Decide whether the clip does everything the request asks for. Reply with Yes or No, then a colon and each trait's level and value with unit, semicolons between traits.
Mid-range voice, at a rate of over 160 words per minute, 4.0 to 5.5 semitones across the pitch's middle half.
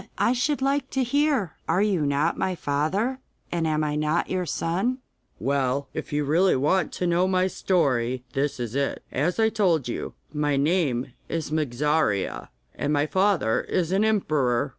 Yes: medium, 160 Hz; average, 170 wpm; average, 5.0 semitones